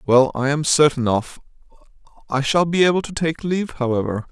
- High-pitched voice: No, medium, 145 Hz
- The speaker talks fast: No, average, 165 wpm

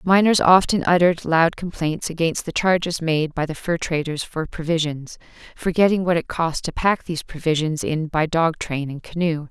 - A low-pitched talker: No, medium, 165 Hz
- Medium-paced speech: Yes, average, 185 wpm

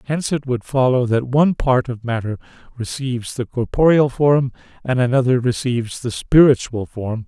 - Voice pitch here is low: Yes, low, 125 Hz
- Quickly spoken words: No, average, 155 wpm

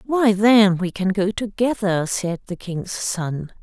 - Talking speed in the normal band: Yes, average, 165 wpm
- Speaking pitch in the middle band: No, high, 200 Hz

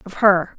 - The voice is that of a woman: Yes, female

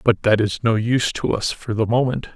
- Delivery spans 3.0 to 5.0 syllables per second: No, 5.4 syllables/s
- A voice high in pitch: No, low, 115 Hz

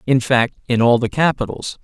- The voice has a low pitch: Yes, low, 125 Hz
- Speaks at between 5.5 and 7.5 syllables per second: No, 5.2 syllables/s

